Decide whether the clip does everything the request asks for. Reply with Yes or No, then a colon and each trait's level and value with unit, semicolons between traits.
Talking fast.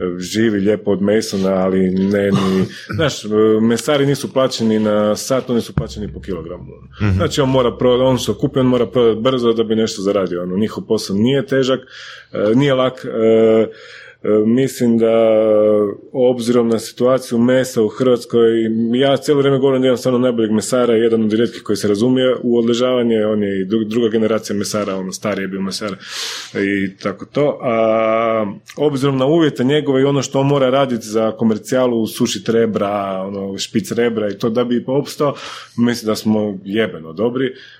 Yes: fast, 170 wpm